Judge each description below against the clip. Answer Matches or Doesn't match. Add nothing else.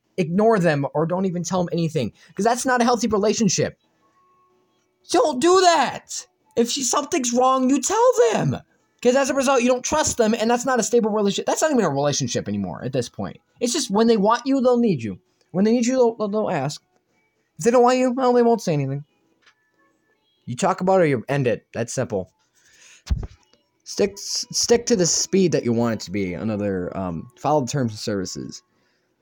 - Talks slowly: Doesn't match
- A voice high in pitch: Matches